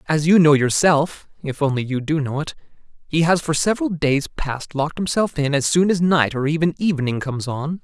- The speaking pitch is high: No, medium, 155 Hz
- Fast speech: Yes, fast, 215 wpm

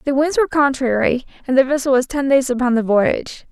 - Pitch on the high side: Yes, very high, 265 Hz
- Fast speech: Yes, fast, 220 wpm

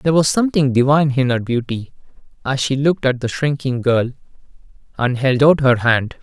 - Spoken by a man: Yes, male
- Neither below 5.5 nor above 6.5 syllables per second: Yes, 5.7 syllables/s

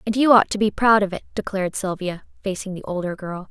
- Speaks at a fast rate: Yes, fast, 240 wpm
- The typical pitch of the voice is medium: No, high, 195 Hz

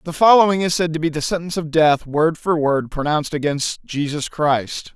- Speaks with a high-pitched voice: No, medium, 155 Hz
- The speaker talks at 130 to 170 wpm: No, fast, 205 wpm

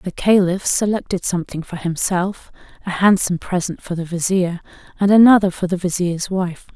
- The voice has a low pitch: No, medium, 185 Hz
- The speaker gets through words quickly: No, average, 160 wpm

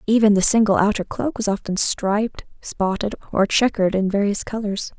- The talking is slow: No, average, 170 wpm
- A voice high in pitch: Yes, high, 205 Hz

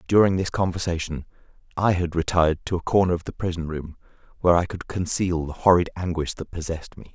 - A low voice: Yes, very low, 85 Hz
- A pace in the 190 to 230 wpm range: Yes, average, 195 wpm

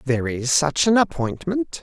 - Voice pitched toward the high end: No, medium, 160 Hz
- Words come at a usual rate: Yes, average, 165 wpm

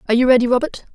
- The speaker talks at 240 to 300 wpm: Yes, fast, 255 wpm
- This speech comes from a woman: Yes, female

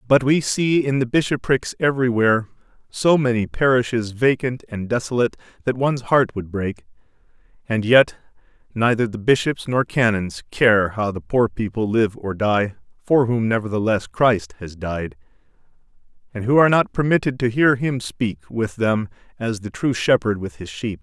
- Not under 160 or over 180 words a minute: Yes, average, 165 wpm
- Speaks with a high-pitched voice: No, low, 115 Hz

